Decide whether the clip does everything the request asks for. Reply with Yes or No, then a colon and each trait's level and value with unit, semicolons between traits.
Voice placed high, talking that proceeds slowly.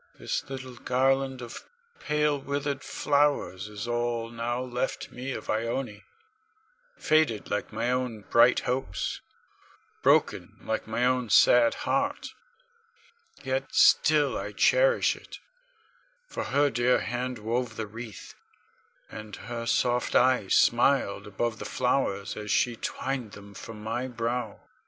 No: low, 120 Hz; slow, 130 wpm